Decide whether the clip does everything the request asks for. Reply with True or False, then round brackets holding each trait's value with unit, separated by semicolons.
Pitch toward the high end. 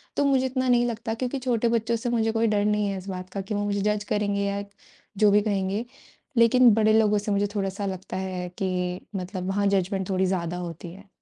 True (205 Hz)